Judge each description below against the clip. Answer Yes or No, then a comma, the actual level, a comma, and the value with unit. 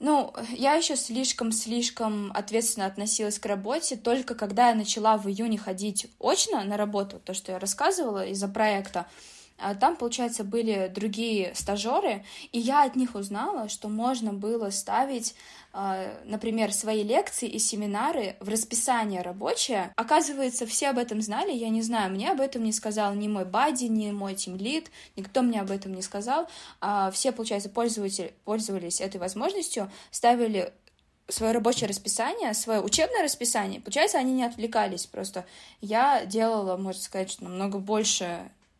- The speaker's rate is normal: Yes, average, 150 wpm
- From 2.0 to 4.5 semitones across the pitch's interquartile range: Yes, average, 3.1 semitones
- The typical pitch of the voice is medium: No, high, 215 Hz